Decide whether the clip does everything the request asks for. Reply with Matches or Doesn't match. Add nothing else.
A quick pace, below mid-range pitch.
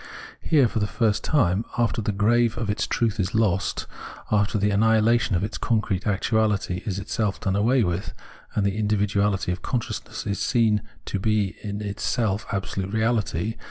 Doesn't match